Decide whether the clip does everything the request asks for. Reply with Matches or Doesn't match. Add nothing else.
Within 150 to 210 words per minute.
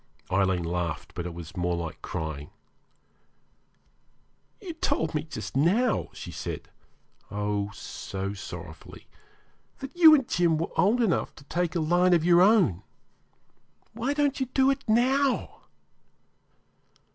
Doesn't match